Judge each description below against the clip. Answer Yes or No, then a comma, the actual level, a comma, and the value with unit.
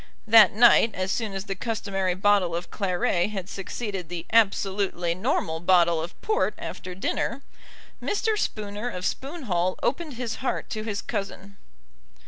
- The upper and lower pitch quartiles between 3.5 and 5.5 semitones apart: Yes, average, 3.8 semitones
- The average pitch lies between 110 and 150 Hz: No, high, 200 Hz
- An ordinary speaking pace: Yes, average, 150 wpm